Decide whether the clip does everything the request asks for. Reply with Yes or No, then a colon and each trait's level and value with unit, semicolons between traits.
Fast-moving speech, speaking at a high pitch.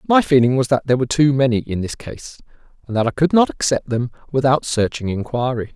No: fast, 220 wpm; low, 130 Hz